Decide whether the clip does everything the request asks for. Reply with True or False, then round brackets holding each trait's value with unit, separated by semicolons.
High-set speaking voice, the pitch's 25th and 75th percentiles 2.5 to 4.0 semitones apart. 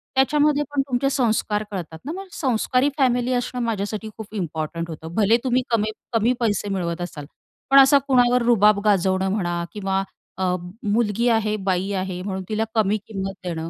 False (215 Hz; 4.5 semitones)